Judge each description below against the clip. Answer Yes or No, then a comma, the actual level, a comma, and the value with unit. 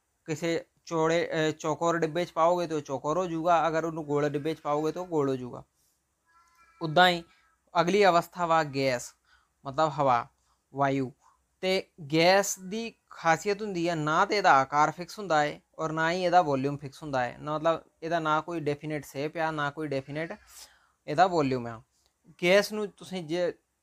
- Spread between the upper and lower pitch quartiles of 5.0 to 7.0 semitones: No, average, 3.2 semitones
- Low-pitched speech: No, medium, 160 Hz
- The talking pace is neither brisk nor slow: No, fast, 170 wpm